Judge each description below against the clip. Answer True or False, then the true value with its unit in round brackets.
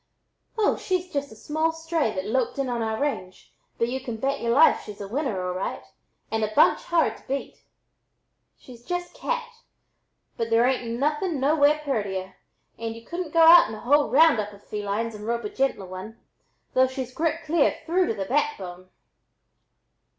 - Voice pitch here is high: True (260 Hz)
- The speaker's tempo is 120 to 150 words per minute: False (185 wpm)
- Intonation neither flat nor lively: False (6.3 semitones)